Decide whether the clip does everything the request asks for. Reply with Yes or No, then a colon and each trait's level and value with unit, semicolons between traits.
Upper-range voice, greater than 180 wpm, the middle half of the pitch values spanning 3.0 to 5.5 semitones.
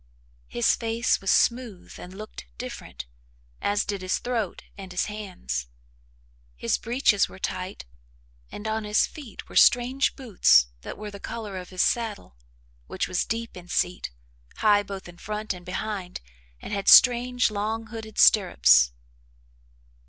No: high, 205 Hz; average, 145 wpm; average, 3.6 semitones